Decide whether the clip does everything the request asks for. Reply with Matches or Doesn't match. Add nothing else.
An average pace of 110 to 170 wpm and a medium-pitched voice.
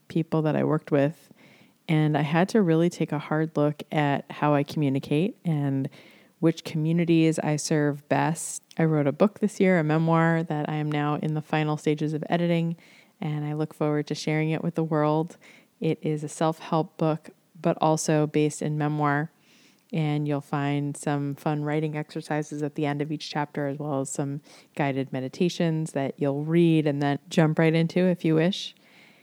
Doesn't match